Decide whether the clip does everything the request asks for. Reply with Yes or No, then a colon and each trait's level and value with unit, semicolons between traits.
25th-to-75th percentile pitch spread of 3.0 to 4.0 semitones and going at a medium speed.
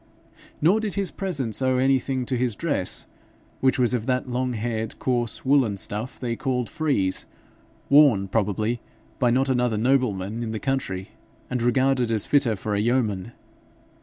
Yes: average, 3.3 semitones; average, 160 wpm